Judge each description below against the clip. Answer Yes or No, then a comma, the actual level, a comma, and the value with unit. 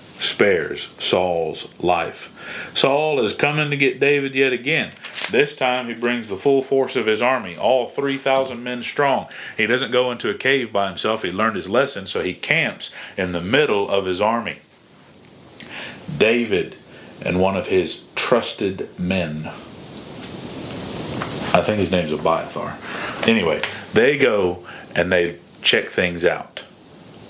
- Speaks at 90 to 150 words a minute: Yes, average, 145 wpm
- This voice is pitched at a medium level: No, low, 120 Hz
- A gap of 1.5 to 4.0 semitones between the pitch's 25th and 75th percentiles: No, wide, 5.6 semitones